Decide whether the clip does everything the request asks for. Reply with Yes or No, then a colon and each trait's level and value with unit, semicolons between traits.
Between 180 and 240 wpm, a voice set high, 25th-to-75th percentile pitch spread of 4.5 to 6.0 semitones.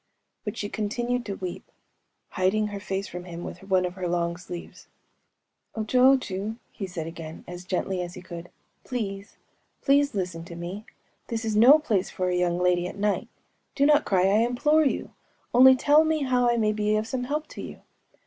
Yes: average, 185 wpm; high, 205 Hz; average, 5.3 semitones